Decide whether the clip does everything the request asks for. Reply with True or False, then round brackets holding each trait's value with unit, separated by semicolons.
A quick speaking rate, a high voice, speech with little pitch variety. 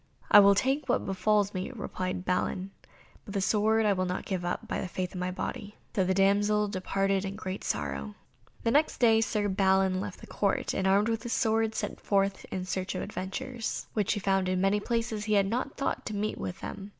True (220 wpm; 200 Hz; 2.3 semitones)